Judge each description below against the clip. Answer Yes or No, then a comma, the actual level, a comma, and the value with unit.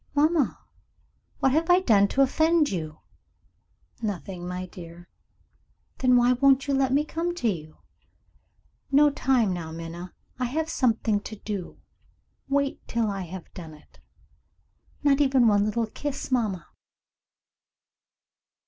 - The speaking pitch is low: No, high, 235 Hz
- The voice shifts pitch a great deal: Yes, wide, 7.1 semitones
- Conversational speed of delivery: No, slow, 130 wpm